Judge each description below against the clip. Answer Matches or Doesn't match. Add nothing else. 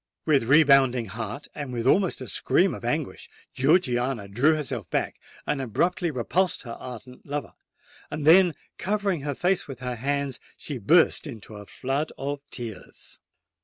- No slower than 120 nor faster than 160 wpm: Matches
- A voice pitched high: Doesn't match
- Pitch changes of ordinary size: Matches